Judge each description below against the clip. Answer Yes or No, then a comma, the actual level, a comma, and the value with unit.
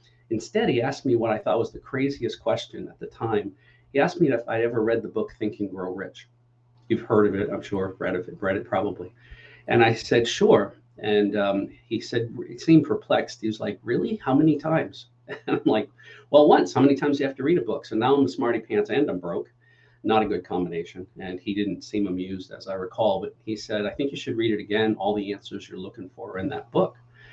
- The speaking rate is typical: No, fast, 245 wpm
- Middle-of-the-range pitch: No, low, 110 Hz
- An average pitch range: Yes, average, 3.2 semitones